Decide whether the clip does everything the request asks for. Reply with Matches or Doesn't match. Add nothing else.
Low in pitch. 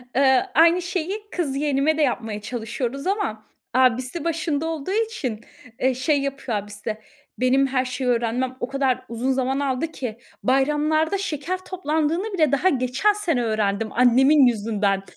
Doesn't match